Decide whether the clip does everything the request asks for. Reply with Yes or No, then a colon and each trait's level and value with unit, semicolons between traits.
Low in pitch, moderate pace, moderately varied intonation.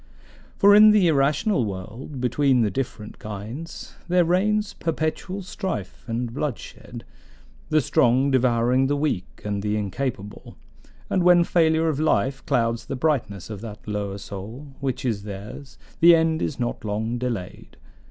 No: low, 130 Hz; average, 145 wpm; wide, 6.9 semitones